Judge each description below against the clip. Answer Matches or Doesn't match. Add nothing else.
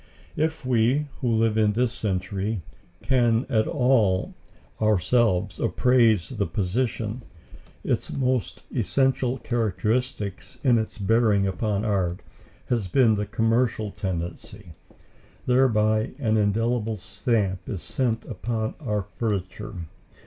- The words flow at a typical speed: Doesn't match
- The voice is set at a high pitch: Doesn't match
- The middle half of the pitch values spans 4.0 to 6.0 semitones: Doesn't match